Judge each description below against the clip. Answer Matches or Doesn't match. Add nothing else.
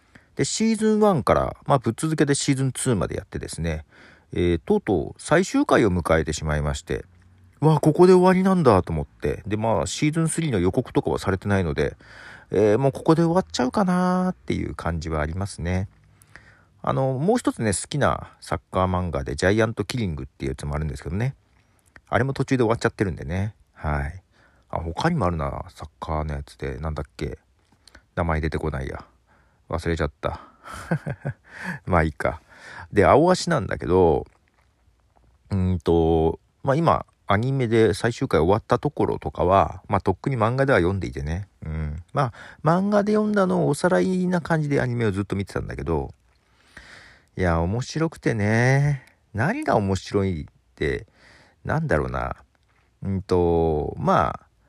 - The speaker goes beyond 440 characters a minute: Doesn't match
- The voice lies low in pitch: Matches